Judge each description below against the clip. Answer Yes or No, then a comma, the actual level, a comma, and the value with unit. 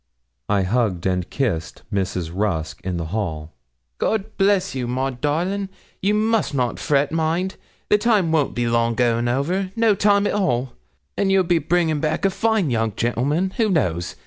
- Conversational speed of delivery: Yes, average, 175 wpm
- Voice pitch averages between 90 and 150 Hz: Yes, medium, 140 Hz